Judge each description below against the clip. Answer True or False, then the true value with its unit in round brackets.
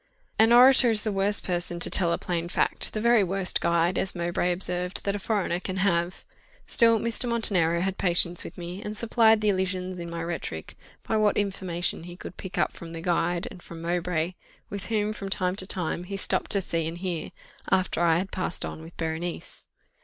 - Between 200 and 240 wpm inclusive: True (205 wpm)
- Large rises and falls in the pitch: False (2.9 semitones)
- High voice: False (180 Hz)